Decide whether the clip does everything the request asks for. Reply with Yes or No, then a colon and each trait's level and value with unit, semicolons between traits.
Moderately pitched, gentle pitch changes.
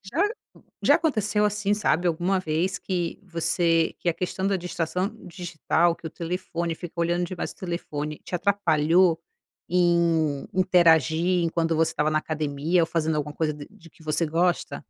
Yes: medium, 170 Hz; narrow, 2.2 semitones